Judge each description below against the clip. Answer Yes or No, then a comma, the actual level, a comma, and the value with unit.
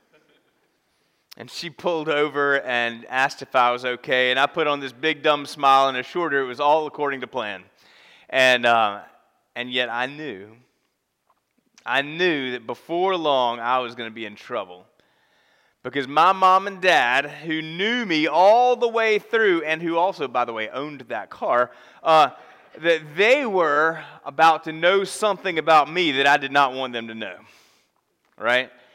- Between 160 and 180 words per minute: Yes, average, 175 wpm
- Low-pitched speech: No, medium, 145 Hz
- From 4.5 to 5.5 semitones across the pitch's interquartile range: Yes, average, 4.9 semitones